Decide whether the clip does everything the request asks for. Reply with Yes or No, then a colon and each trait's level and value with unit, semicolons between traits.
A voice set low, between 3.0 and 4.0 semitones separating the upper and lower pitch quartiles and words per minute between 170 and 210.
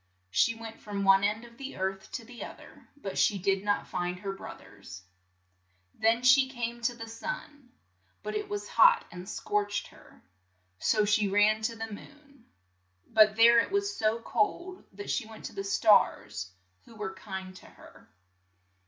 No: high, 220 Hz; average, 3.3 semitones; average, 180 wpm